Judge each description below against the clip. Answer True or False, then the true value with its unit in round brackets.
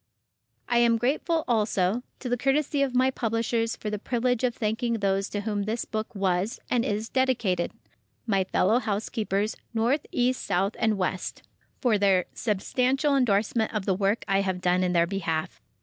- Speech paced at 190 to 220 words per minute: False (165 wpm)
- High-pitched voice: True (220 Hz)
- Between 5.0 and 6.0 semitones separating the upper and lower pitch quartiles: False (3.9 semitones)